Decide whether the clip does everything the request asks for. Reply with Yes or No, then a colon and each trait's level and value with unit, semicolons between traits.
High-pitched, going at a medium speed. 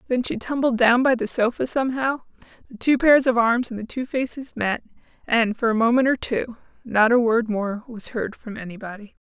No: high, 235 Hz; fast, 210 wpm